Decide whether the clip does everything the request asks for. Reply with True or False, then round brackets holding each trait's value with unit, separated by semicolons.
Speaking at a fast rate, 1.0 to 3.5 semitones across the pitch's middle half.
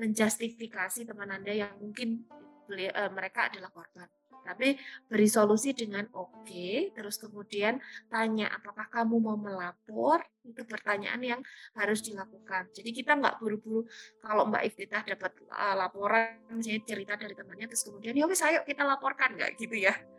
True (150 wpm; 2.7 semitones)